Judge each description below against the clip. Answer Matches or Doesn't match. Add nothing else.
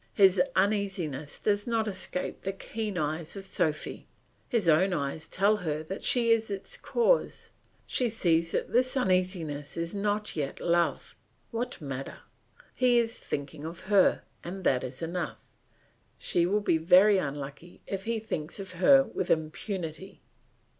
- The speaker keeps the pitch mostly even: Doesn't match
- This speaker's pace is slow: Doesn't match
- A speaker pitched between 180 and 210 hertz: Matches